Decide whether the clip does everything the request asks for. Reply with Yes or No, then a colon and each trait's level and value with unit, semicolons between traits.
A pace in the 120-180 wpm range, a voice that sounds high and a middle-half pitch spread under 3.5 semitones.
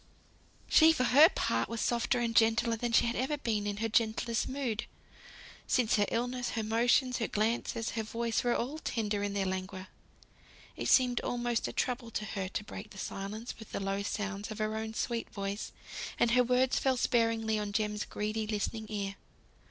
No: average, 190 wpm; high, 225 Hz; narrow, 2.5 semitones